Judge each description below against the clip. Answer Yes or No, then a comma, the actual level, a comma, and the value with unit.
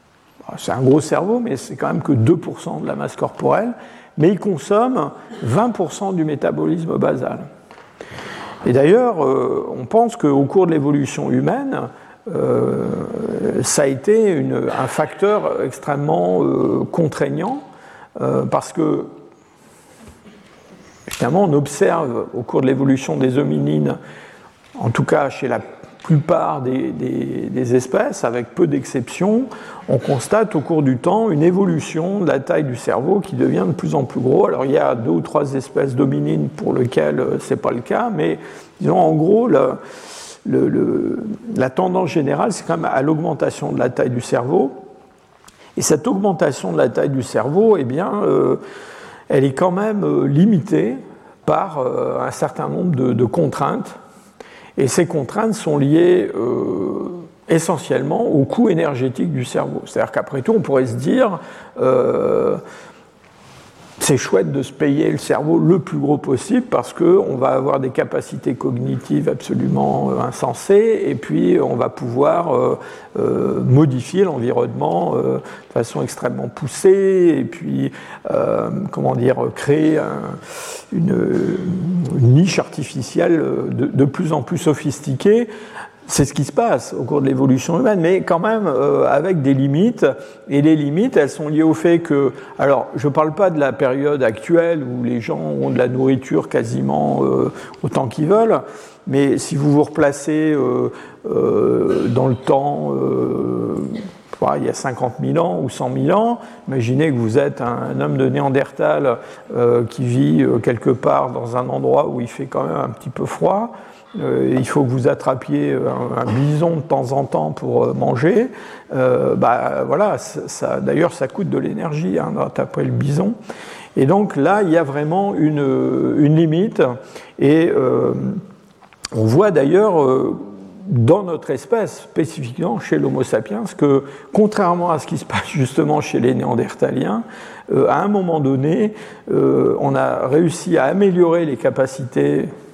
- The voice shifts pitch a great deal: Yes, wide, 7.4 semitones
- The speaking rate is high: No, average, 155 wpm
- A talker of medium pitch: Yes, medium, 155 Hz